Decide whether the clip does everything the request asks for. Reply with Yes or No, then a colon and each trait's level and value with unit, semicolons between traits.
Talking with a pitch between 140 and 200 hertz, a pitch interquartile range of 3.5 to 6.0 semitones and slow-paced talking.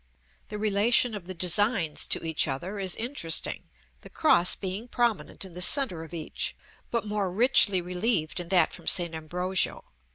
No: medium, 185 Hz; average, 3.8 semitones; average, 165 wpm